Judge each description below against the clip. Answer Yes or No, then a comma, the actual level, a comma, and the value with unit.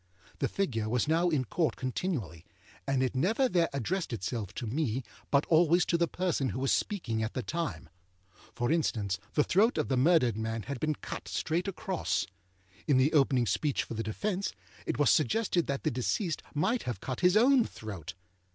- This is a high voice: No, medium, 140 Hz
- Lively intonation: Yes, wide, 6.7 semitones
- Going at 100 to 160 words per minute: No, average, 190 wpm